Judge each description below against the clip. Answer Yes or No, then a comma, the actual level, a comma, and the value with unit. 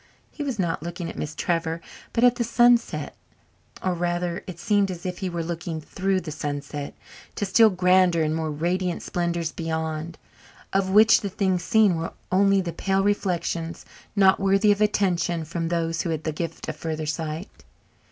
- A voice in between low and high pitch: Yes, medium, 175 Hz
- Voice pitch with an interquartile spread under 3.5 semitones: Yes, average, 3.1 semitones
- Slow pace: No, average, 180 wpm